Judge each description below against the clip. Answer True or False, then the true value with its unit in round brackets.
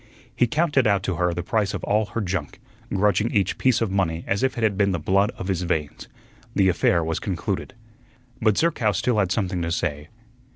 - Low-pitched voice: True (95 Hz)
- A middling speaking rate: False (210 wpm)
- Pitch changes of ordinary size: True (3.6 semitones)